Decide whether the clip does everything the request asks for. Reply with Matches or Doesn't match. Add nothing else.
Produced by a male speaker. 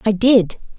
Doesn't match